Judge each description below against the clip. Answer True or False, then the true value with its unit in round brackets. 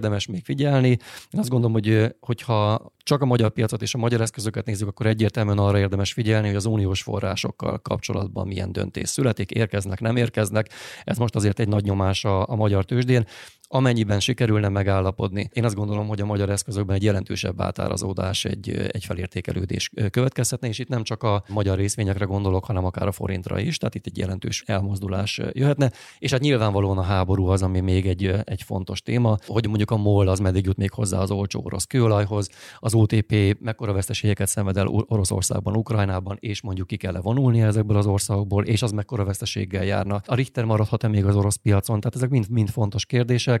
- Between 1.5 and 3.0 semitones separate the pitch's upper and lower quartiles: True (2.5 semitones)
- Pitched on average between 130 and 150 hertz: False (105 Hz)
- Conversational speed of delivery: False (190 wpm)